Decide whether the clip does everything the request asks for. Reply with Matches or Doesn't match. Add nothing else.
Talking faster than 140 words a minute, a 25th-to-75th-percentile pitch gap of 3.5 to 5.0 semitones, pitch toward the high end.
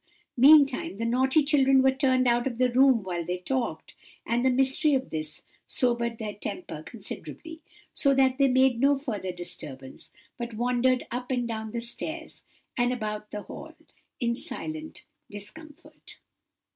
Doesn't match